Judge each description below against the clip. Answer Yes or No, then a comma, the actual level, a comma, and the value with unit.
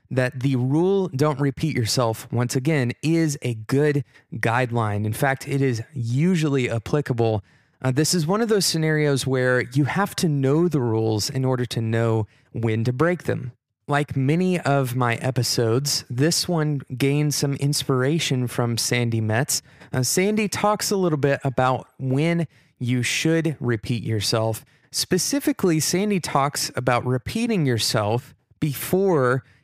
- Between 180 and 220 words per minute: No, average, 145 wpm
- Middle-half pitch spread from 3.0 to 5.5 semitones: Yes, average, 4.0 semitones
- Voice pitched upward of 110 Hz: Yes, low, 135 Hz